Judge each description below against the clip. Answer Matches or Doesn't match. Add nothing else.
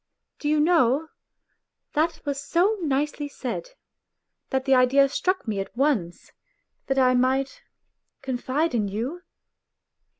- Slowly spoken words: Matches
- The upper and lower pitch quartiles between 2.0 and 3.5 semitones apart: Matches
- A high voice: Matches